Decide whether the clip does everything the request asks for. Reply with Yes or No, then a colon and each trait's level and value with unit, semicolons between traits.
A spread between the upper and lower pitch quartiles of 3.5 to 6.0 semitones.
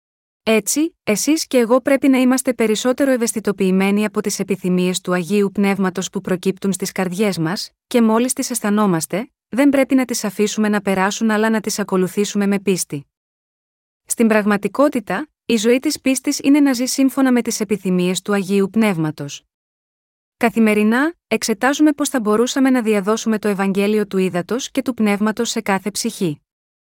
Yes: average, 4.3 semitones